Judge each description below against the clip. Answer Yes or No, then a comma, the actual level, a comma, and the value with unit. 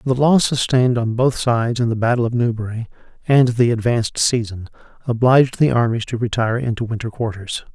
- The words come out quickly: No, average, 180 wpm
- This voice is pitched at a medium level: No, low, 120 Hz